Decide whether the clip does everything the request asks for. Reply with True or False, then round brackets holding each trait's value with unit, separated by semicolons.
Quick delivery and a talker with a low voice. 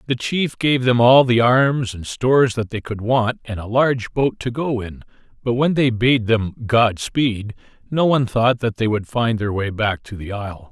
True (225 wpm; 115 Hz)